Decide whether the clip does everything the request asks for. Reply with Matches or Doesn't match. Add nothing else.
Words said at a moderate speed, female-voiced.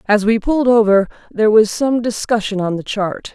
Matches